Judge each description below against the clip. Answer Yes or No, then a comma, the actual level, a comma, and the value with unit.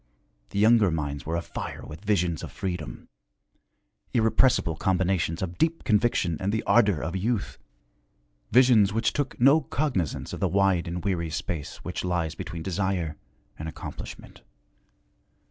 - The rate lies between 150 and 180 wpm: No, average, 140 wpm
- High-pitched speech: No, very low, 95 Hz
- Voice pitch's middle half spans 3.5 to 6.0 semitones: Yes, average, 4.6 semitones